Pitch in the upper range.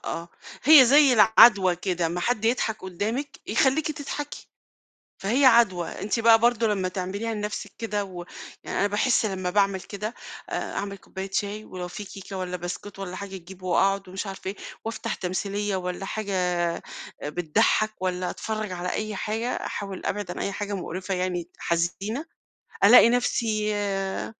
Yes: high, 200 Hz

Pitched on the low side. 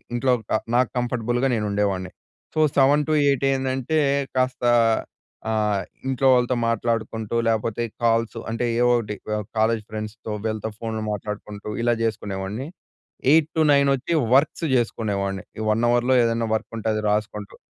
Yes: low, 115 Hz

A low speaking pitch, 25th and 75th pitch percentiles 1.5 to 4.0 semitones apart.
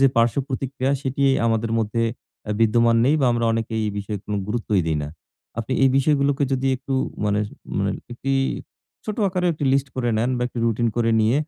Yes: low, 120 Hz; average, 3.3 semitones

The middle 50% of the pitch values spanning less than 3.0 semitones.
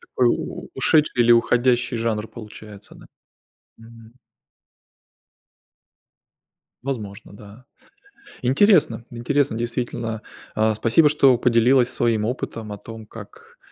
Yes: narrow, 2.5 semitones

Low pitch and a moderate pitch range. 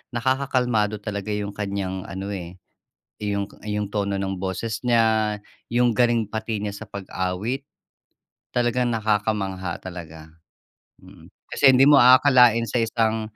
Yes: low, 105 Hz; average, 3.3 semitones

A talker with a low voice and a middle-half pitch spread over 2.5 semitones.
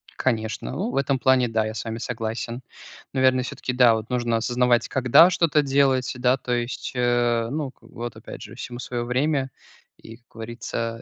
No: low, 125 Hz; narrow, 2.0 semitones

